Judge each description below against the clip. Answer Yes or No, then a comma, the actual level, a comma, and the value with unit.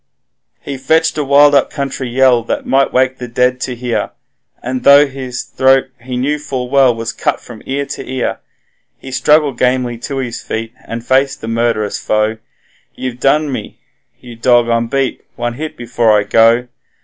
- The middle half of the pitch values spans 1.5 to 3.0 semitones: Yes, narrow, 2.5 semitones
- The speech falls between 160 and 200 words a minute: Yes, average, 180 wpm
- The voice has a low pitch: Yes, low, 125 Hz